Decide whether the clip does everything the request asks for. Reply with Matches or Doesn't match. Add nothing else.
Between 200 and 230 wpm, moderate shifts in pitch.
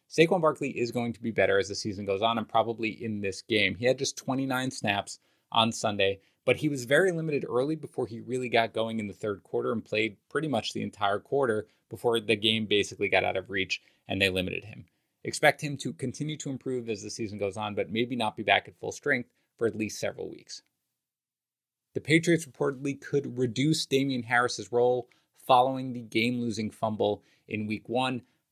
Matches